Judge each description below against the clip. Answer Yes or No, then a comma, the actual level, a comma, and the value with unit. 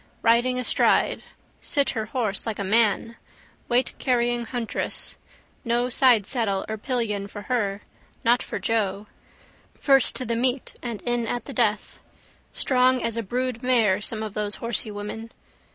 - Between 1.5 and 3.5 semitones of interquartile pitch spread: Yes, average, 2.8 semitones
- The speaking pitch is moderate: No, high, 230 Hz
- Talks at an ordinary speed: Yes, average, 145 wpm